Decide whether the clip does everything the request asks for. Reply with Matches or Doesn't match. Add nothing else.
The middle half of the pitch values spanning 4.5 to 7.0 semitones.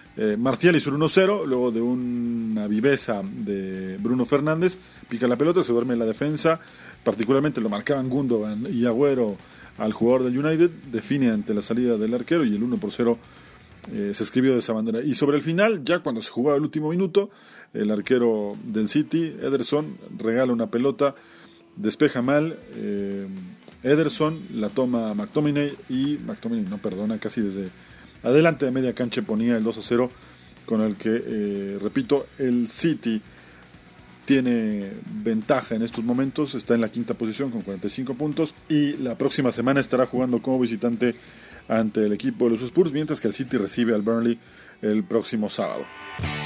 Matches